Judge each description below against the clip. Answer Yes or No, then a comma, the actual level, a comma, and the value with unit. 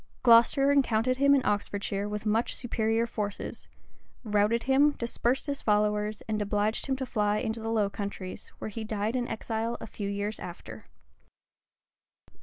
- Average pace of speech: Yes, average, 155 wpm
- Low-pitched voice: No, high, 220 Hz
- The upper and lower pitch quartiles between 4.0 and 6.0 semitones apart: No, narrow, 2.4 semitones